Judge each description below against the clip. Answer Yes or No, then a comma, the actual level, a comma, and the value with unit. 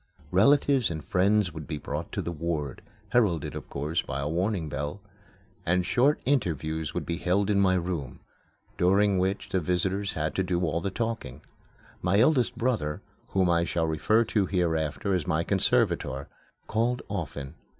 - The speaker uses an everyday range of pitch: Yes, average, 4.4 semitones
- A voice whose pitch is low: Yes, very low, 90 Hz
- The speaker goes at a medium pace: Yes, average, 165 wpm